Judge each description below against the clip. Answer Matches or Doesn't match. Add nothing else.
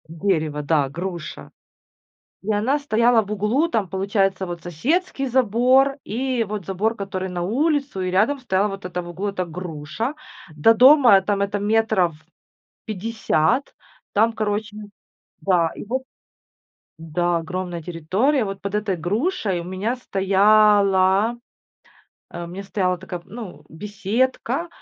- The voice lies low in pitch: Doesn't match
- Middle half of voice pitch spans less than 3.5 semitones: Doesn't match